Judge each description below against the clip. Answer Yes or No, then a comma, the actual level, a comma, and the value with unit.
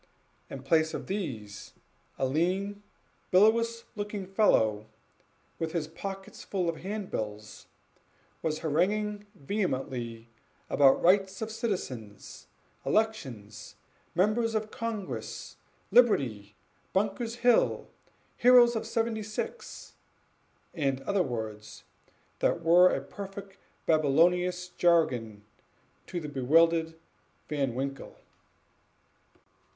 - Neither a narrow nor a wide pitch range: No, wide, 7.5 semitones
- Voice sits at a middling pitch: Yes, medium, 175 Hz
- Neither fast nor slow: No, slow, 95 wpm